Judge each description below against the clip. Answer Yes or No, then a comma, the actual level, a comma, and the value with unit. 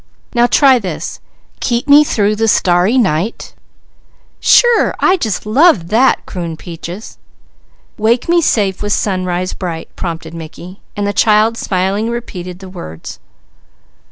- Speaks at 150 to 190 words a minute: No, slow, 135 wpm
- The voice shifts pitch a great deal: No, average, 4.9 semitones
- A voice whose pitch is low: No, high, 205 Hz